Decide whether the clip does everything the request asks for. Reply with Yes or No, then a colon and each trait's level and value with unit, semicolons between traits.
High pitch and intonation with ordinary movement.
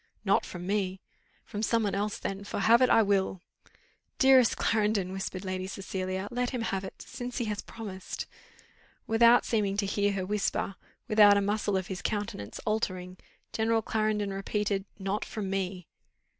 No: high, 205 Hz; narrow, 2.2 semitones